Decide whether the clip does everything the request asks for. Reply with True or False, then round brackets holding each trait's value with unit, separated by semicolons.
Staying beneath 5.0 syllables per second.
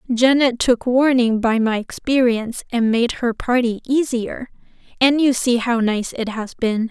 True (4.3 syllables/s)